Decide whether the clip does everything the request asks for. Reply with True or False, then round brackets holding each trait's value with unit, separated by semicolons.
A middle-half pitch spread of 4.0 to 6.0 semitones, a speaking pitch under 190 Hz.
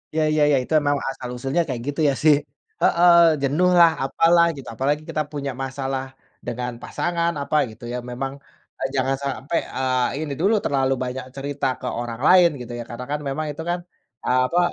False (3.3 semitones; 140 Hz)